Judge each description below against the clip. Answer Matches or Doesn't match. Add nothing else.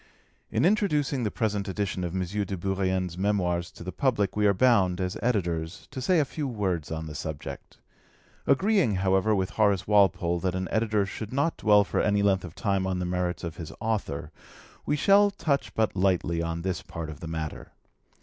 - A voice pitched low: Matches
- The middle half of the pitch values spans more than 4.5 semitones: Doesn't match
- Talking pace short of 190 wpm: Doesn't match